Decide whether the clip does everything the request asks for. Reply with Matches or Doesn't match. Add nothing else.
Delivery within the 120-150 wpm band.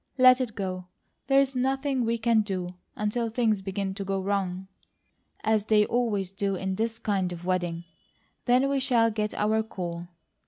Doesn't match